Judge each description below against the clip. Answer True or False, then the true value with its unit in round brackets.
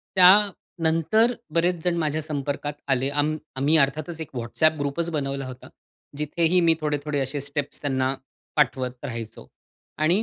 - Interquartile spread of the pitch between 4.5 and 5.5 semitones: False (3.0 semitones)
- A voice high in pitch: False (150 Hz)